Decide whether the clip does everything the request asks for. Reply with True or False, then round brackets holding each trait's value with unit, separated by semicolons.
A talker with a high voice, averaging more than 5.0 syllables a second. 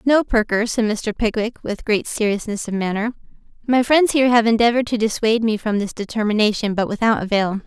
True (220 Hz; 5.9 syllables/s)